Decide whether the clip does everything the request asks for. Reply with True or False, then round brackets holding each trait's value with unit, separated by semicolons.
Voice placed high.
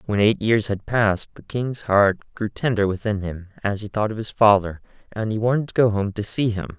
False (105 Hz)